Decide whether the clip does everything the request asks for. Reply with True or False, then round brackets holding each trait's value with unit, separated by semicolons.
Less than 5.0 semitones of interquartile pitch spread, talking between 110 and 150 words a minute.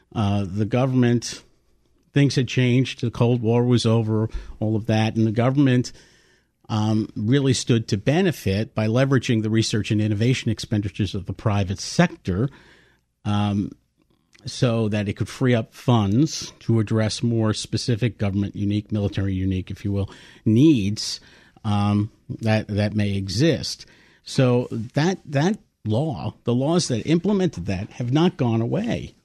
True (3.6 semitones; 145 wpm)